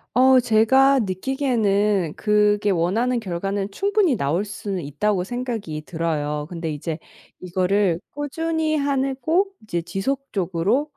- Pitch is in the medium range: No, high, 210 Hz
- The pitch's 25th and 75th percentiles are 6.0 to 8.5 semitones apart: Yes, wide, 6.9 semitones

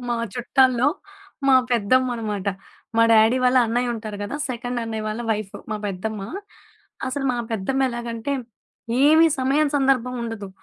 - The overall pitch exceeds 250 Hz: No, high, 240 Hz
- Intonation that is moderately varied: Yes, average, 3.0 semitones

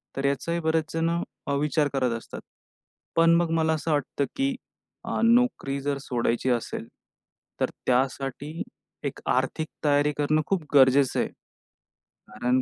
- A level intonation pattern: No, average, 3.3 semitones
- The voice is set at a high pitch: No, medium, 145 Hz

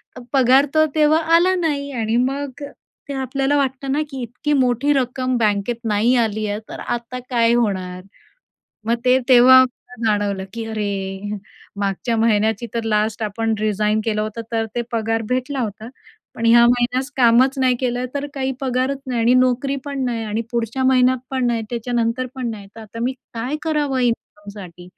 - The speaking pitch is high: Yes, high, 240 Hz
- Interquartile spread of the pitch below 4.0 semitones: Yes, average, 3.0 semitones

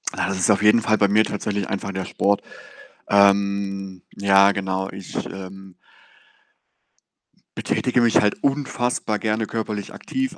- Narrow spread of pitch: Yes, narrow, 1.8 semitones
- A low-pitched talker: Yes, low, 100 Hz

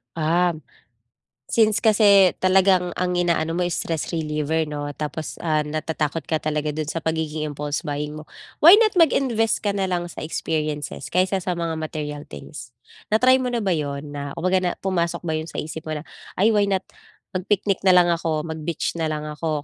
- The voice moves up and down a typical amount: Yes, average, 3.5 semitones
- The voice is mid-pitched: Yes, medium, 165 Hz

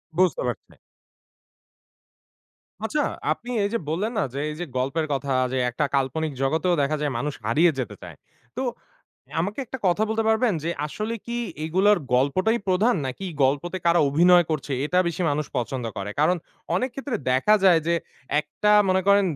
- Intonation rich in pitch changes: Yes, wide, 6.5 semitones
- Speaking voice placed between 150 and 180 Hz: Yes, medium, 170 Hz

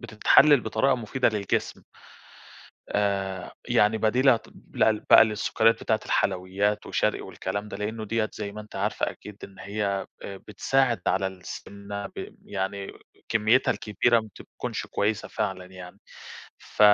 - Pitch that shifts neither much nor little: No, narrow, 2.0 semitones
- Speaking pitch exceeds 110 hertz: No, low, 105 Hz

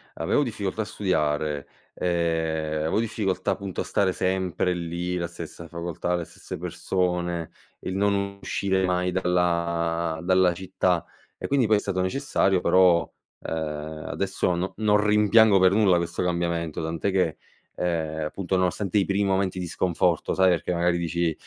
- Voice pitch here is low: Yes, very low, 90 Hz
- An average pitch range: No, narrow, 2.3 semitones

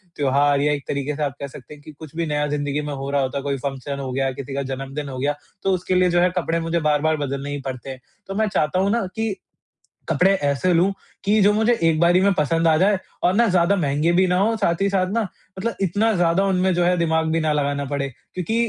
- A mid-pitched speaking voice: Yes, medium, 160 Hz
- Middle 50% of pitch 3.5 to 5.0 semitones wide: Yes, average, 4.6 semitones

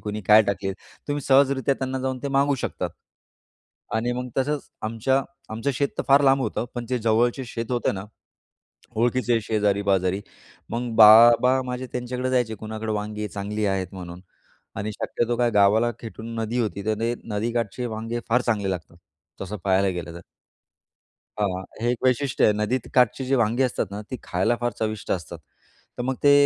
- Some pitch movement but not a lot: Yes, average, 3.2 semitones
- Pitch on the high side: No, low, 115 Hz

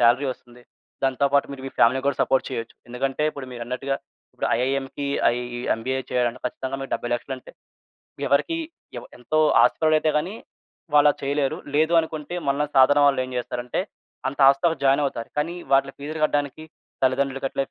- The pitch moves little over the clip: Yes, narrow, 2.1 semitones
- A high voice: No, low, 135 Hz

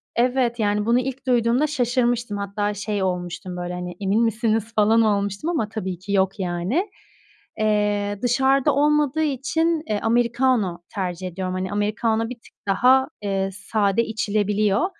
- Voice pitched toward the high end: Yes, high, 215 Hz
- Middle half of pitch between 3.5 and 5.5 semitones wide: Yes, average, 3.8 semitones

